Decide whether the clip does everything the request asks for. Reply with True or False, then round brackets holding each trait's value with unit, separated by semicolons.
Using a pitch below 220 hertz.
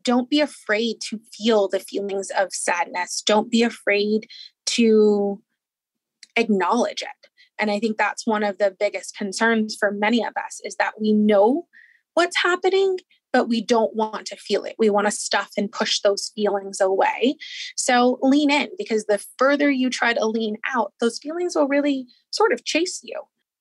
False (225 Hz)